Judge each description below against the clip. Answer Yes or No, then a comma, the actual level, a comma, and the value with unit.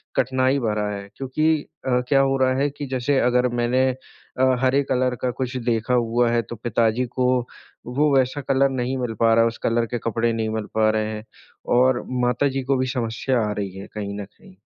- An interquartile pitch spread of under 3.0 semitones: Yes, narrow, 2.5 semitones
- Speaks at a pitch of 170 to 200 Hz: No, low, 125 Hz